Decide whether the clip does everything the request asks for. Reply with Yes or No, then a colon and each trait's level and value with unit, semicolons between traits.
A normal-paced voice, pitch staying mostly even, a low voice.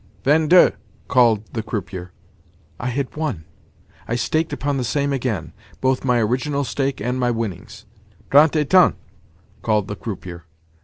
No: average, 145 wpm; average, 4.9 semitones; low, 125 Hz